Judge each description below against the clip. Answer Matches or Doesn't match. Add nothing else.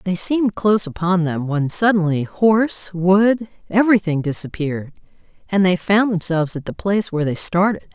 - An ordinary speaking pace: Matches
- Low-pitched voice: Doesn't match